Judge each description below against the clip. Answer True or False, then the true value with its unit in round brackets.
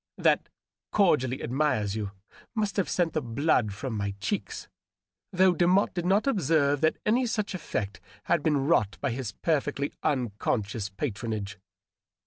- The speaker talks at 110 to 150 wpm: True (145 wpm)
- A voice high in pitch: False (140 Hz)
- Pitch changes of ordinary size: False (8.3 semitones)